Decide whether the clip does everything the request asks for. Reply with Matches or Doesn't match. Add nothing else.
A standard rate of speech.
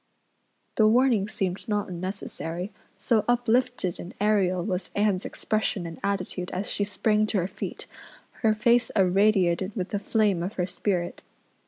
Matches